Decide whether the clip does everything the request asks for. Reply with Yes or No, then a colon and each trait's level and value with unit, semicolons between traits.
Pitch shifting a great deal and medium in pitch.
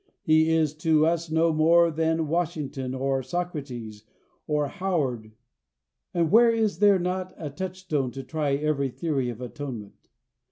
No: average, 3.9 semitones; medium, 155 Hz